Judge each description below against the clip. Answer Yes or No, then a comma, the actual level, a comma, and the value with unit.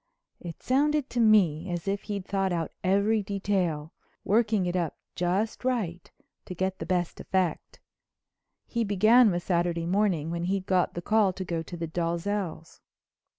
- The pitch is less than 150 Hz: No, medium, 185 Hz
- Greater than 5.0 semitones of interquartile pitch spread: No, average, 3.2 semitones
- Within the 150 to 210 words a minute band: Yes, average, 160 wpm